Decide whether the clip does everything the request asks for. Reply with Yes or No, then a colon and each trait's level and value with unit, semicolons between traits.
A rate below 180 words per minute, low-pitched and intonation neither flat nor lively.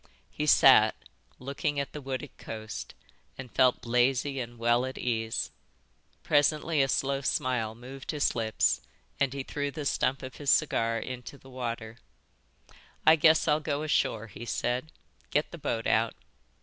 Yes: average, 155 wpm; low, 130 Hz; average, 3.5 semitones